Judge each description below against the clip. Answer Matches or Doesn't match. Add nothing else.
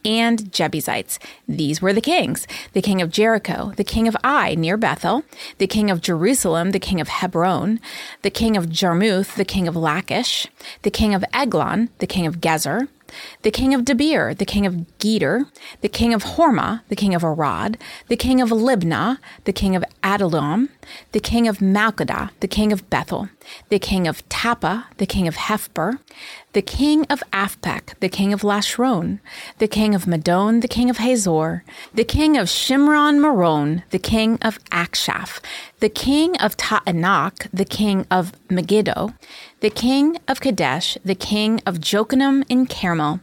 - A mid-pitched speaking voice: Doesn't match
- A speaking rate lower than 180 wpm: Matches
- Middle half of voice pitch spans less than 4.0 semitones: Doesn't match